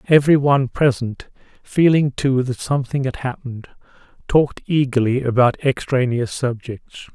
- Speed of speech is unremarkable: No, slow, 110 wpm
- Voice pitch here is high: No, low, 130 Hz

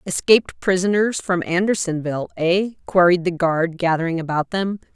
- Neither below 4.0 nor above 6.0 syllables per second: Yes, 5.1 syllables/s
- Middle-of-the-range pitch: Yes, medium, 180 Hz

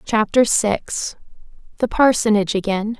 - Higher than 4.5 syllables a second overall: No, 4.4 syllables/s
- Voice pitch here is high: Yes, high, 215 Hz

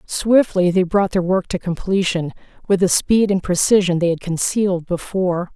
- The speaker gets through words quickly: No, average, 175 wpm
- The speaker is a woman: Yes, female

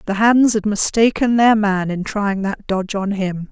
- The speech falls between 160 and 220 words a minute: Yes, fast, 205 wpm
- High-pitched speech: Yes, high, 205 Hz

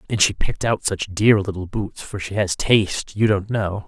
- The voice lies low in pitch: Yes, low, 100 Hz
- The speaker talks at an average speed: No, fast, 235 wpm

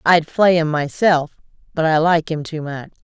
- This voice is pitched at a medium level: Yes, medium, 160 Hz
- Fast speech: No, average, 195 wpm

